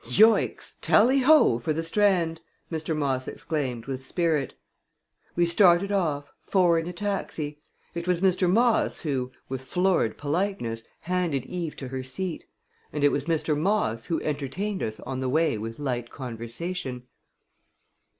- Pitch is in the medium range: Yes, medium, 160 Hz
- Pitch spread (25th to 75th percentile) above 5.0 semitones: Yes, wide, 5.5 semitones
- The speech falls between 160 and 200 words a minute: No, average, 150 wpm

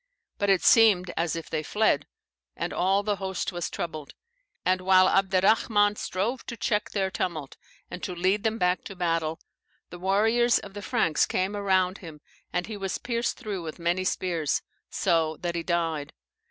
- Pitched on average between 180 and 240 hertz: Yes, medium, 185 Hz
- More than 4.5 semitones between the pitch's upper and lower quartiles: No, average, 3.1 semitones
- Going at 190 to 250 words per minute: No, average, 175 wpm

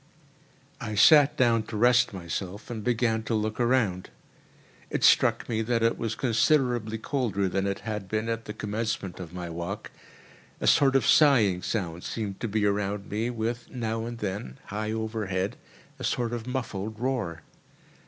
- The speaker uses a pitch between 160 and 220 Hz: No, low, 110 Hz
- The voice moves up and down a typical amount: Yes, average, 3.1 semitones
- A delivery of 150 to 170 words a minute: Yes, average, 165 wpm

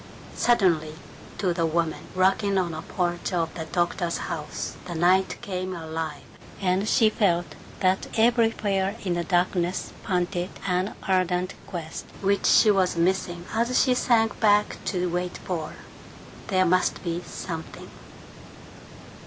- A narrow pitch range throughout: Yes, narrow, 2.3 semitones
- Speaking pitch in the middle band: Yes, medium, 180 Hz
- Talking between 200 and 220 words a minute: No, slow, 135 wpm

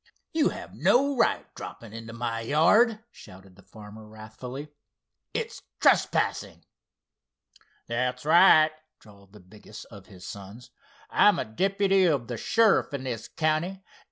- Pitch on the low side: Yes, low, 125 Hz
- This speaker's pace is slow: Yes, slow, 130 wpm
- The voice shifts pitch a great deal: Yes, wide, 8.4 semitones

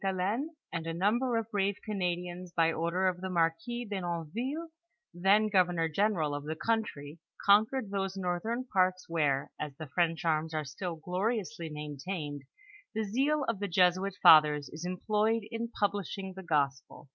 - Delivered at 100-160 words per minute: Yes, average, 155 wpm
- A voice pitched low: No, medium, 185 Hz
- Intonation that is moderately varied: Yes, average, 4.4 semitones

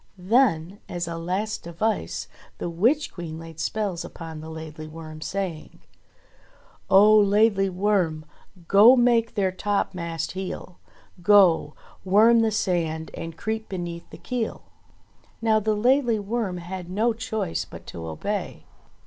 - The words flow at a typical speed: No, slow, 130 wpm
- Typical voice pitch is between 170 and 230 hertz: Yes, high, 190 Hz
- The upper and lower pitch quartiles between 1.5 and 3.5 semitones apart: No, average, 4.6 semitones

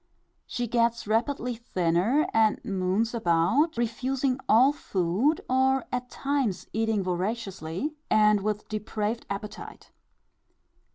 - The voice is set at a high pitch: Yes, high, 225 Hz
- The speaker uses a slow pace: Yes, slow, 105 wpm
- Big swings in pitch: No, average, 4.1 semitones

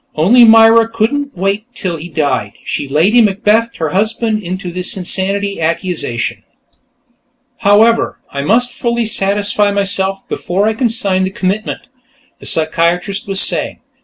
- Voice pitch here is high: Yes, high, 200 Hz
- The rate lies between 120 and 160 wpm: Yes, average, 140 wpm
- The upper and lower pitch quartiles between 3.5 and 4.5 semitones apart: Yes, average, 3.8 semitones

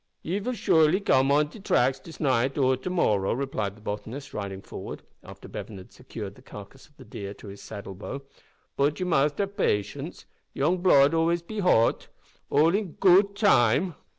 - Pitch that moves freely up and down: Yes, wide, 8.1 semitones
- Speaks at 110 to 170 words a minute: No, average, 190 wpm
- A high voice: No, medium, 140 Hz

